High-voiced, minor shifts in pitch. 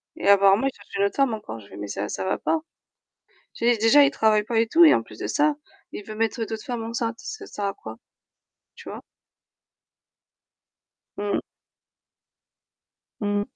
No: high, 220 Hz; average, 3.2 semitones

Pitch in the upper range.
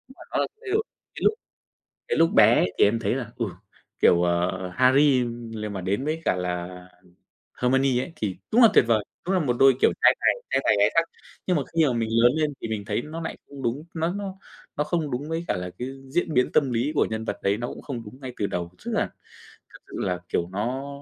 No: low, 125 Hz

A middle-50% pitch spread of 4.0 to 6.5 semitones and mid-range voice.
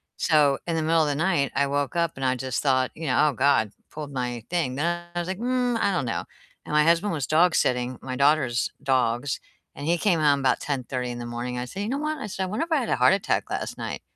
Yes: average, 5.1 semitones; medium, 145 Hz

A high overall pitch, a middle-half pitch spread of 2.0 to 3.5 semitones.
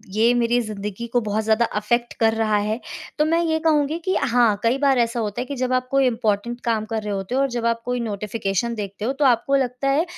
Yes: high, 235 Hz; average, 3.1 semitones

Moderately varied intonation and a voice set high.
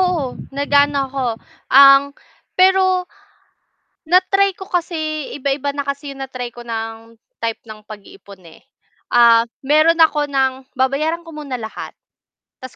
Yes: average, 3.9 semitones; very high, 280 Hz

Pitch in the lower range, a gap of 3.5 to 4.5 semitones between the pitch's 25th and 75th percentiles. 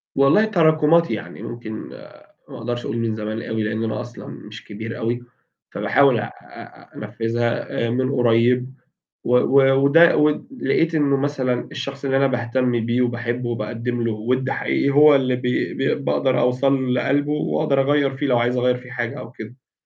No: low, 125 Hz; average, 2.7 semitones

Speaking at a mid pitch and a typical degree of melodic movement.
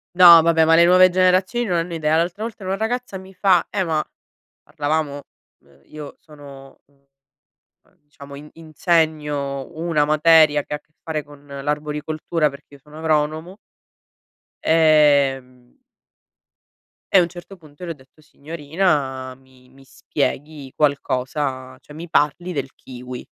Yes: medium, 150 Hz; average, 3.2 semitones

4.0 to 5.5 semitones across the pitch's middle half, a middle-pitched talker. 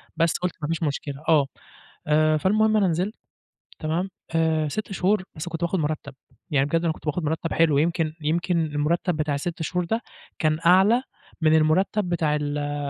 No: average, 2.8 semitones; medium, 160 Hz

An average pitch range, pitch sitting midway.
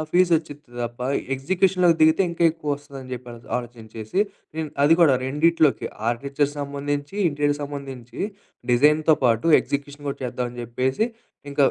Yes: average, 3.6 semitones; medium, 145 Hz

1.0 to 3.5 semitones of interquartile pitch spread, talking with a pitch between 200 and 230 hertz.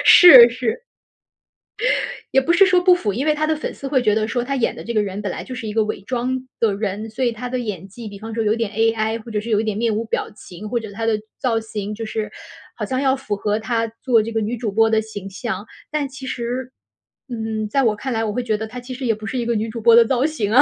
Yes: average, 2.9 semitones; high, 225 Hz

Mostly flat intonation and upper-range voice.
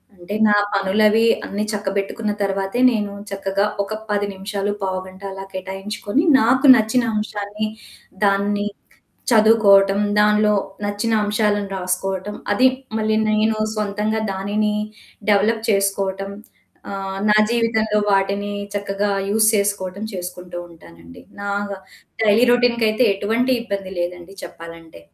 Yes: narrow, 1.8 semitones; high, 205 Hz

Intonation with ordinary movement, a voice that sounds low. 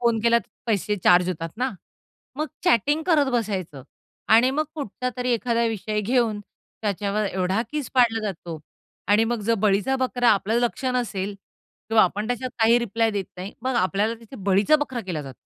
No: average, 3.7 semitones; high, 225 Hz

